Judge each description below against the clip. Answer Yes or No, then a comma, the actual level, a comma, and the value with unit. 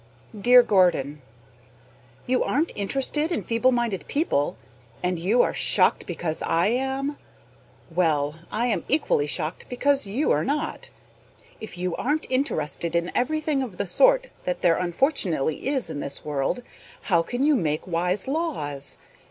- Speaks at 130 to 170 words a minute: Yes, average, 145 wpm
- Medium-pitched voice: No, high, 205 Hz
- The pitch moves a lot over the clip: Yes, wide, 8.4 semitones